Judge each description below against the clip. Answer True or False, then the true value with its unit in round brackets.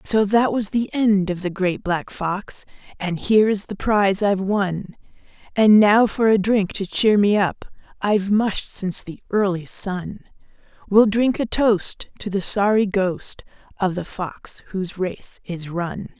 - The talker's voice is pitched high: True (200 Hz)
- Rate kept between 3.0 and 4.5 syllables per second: True (4.1 syllables/s)